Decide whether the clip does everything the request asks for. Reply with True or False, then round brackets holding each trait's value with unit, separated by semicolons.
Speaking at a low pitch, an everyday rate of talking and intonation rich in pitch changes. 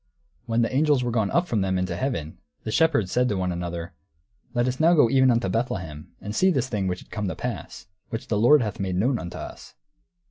False (115 Hz; 235 wpm; 5.7 semitones)